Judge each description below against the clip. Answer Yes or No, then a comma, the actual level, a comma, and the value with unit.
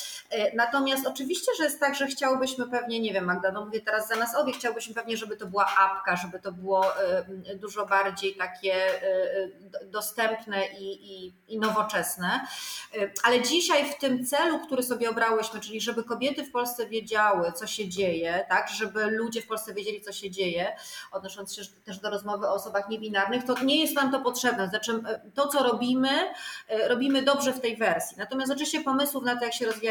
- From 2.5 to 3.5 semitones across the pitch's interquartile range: No, average, 4.8 semitones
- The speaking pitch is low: No, high, 225 Hz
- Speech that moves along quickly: Yes, fast, 180 wpm